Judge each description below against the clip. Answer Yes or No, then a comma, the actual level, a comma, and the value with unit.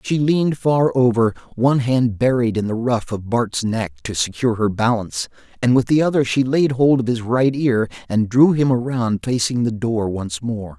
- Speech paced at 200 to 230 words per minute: Yes, fast, 205 wpm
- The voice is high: No, low, 120 Hz